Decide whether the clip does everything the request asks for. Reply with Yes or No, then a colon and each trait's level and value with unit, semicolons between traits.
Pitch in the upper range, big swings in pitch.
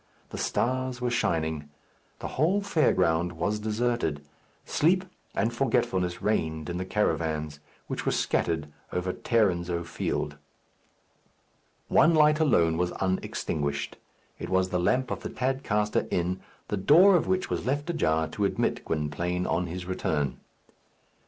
No: very low, 95 Hz; wide, 7.4 semitones